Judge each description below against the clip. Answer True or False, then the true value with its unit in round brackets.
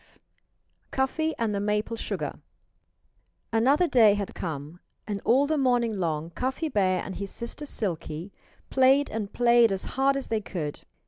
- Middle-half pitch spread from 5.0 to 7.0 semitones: True (5.4 semitones)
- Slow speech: False (155 wpm)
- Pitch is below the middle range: False (225 Hz)